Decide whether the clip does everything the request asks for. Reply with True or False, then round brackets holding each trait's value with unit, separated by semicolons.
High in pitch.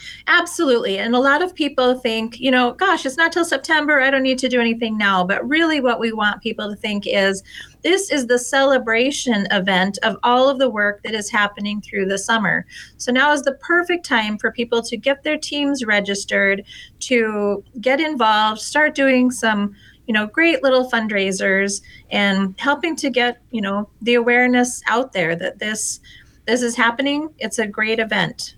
True (235 Hz)